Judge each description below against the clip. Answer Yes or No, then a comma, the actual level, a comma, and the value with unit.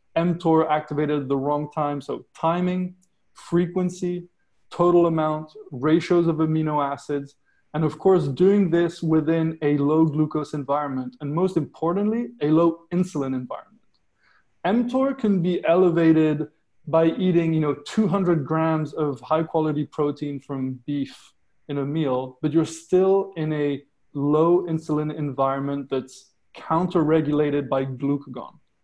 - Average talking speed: No, slow, 130 wpm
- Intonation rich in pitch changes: No, average, 2.9 semitones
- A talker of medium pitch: Yes, medium, 155 Hz